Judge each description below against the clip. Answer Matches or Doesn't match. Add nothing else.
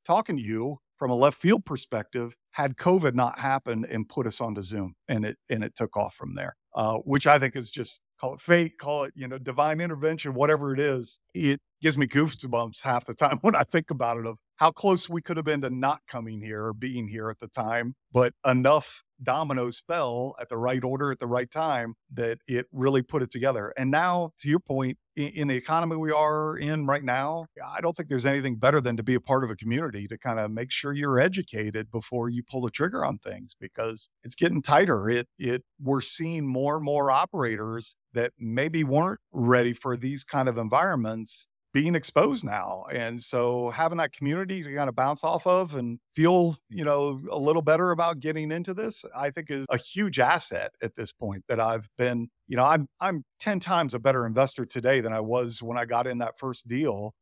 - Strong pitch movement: Doesn't match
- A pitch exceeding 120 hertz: Matches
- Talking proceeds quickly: Matches